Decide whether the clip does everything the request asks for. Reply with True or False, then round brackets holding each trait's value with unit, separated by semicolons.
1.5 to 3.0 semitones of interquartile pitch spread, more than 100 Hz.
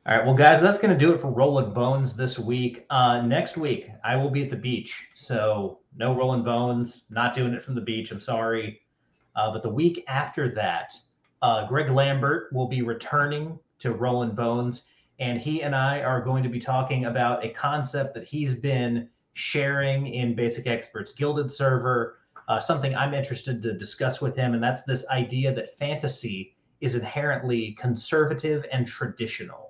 True (2.6 semitones; 130 Hz)